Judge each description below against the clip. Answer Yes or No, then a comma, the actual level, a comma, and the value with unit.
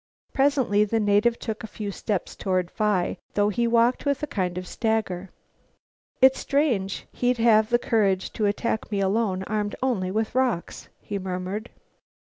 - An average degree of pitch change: Yes, average, 3.4 semitones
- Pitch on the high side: Yes, high, 215 Hz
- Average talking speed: Yes, average, 160 wpm